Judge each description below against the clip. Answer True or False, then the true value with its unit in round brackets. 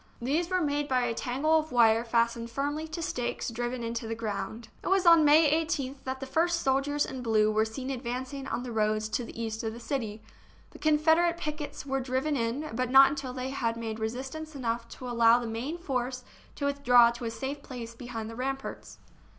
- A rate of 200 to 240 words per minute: True (205 wpm)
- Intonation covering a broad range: False (3.7 semitones)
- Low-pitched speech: False (255 Hz)